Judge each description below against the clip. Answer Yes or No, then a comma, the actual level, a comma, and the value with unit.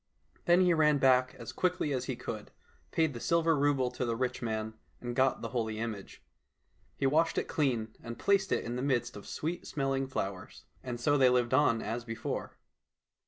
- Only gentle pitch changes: No, average, 3.8 semitones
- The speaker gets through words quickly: No, average, 195 wpm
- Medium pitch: No, low, 130 Hz